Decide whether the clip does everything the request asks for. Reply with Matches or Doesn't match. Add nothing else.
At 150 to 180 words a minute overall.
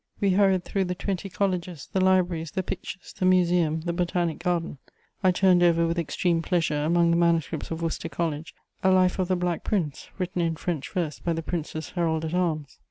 Doesn't match